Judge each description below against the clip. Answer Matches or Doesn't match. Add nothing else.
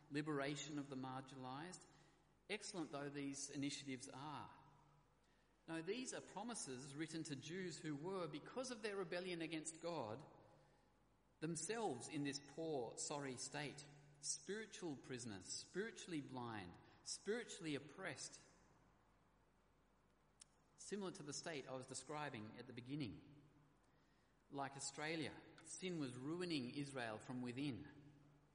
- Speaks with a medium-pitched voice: Matches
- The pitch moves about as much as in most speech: Matches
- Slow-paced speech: Matches